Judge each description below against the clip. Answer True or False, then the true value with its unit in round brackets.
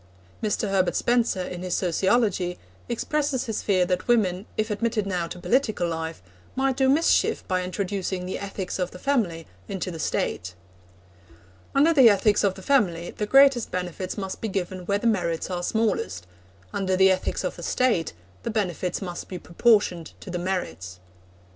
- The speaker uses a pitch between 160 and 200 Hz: True (190 Hz)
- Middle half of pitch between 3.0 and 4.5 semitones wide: True (4.0 semitones)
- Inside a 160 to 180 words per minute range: True (170 wpm)